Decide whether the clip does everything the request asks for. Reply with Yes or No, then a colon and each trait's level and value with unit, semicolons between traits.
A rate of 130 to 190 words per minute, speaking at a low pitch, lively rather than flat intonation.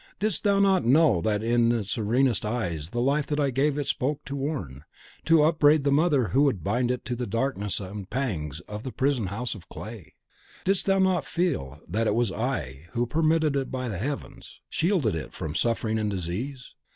No: average, 200 wpm; low, 125 Hz; wide, 5.7 semitones